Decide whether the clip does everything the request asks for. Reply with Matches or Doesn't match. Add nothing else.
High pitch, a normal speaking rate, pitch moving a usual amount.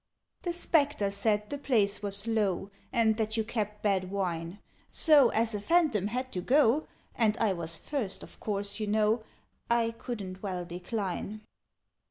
Matches